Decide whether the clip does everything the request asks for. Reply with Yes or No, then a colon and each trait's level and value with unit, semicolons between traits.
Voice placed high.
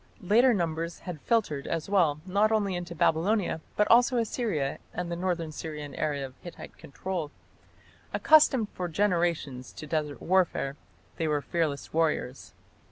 No: medium, 170 Hz